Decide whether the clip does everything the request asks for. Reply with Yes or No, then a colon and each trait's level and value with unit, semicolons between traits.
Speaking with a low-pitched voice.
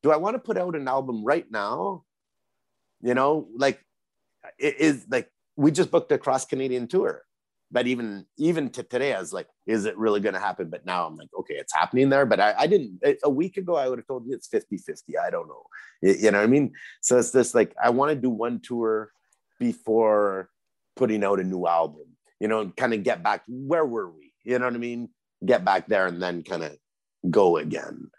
Yes: low, 125 Hz